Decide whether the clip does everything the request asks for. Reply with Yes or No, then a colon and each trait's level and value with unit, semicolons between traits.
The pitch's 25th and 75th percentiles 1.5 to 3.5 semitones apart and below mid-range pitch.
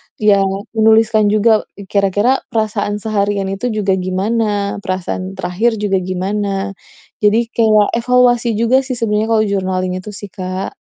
No: narrow, 2.4 semitones; high, 210 Hz